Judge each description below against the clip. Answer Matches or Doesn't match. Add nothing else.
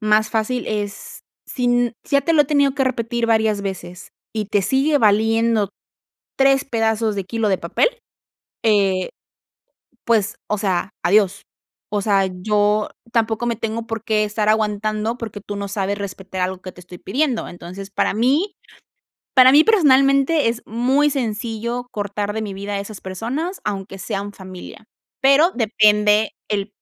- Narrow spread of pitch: Doesn't match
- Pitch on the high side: Matches